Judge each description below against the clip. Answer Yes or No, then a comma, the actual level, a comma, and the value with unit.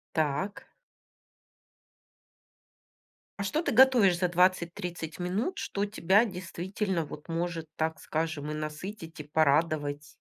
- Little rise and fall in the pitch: No, average, 3.7 semitones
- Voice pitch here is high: No, medium, 175 Hz